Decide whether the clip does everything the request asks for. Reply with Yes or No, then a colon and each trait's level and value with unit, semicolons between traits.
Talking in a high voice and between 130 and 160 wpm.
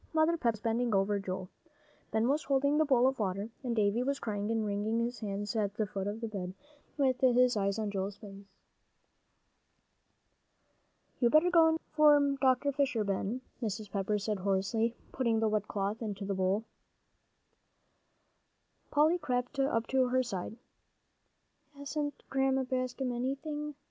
Yes: high, 230 Hz; average, 155 wpm